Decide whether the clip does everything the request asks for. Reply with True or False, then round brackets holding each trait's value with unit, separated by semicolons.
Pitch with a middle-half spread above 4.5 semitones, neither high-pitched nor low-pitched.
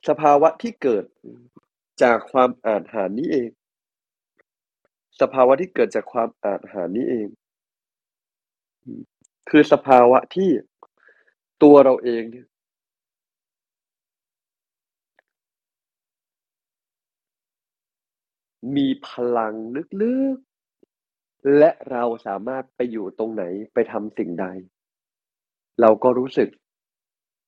False (5.0 semitones; 130 Hz)